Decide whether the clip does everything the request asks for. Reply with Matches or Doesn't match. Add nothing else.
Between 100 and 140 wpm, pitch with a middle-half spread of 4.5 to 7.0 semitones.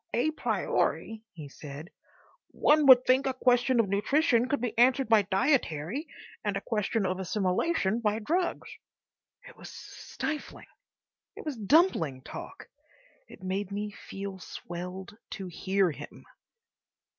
Matches